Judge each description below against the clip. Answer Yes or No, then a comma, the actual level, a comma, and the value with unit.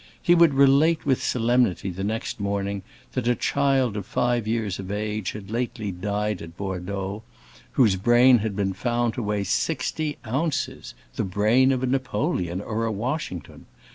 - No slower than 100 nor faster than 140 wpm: No, average, 160 wpm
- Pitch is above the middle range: No, low, 110 Hz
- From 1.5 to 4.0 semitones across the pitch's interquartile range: No, average, 4.4 semitones